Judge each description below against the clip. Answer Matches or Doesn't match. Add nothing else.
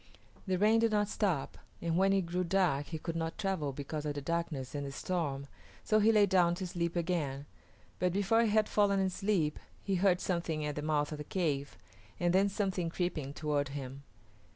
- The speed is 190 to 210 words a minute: Matches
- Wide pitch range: Doesn't match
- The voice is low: Doesn't match